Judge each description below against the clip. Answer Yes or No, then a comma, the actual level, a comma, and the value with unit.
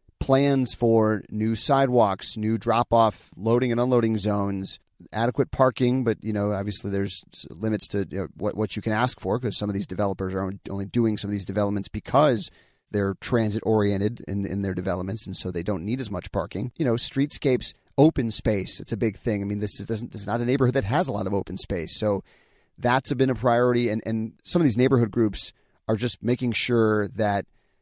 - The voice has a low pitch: Yes, low, 110 Hz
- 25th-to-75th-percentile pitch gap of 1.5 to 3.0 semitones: No, average, 3.4 semitones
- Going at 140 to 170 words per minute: No, fast, 205 wpm